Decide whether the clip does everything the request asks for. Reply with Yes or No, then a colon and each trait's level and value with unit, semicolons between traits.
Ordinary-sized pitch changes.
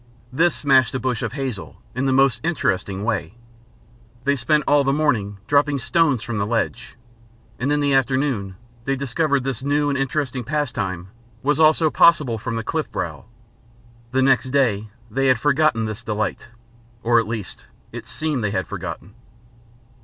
Yes: average, 4.2 semitones